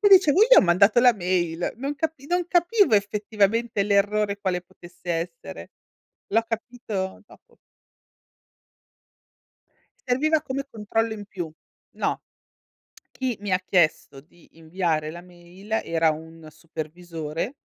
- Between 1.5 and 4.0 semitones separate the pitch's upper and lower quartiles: No, wide, 5.8 semitones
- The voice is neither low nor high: No, high, 200 Hz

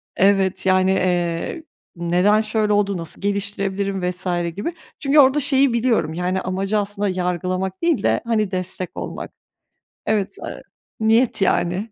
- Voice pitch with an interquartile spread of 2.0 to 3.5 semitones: Yes, average, 2.8 semitones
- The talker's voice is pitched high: Yes, high, 195 Hz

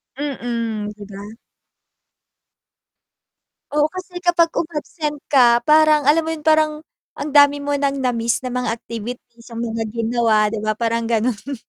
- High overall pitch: Yes, very high, 250 Hz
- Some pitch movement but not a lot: Yes, average, 4.6 semitones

